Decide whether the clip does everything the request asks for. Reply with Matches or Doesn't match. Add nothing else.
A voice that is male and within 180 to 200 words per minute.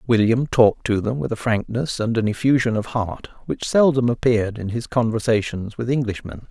Matches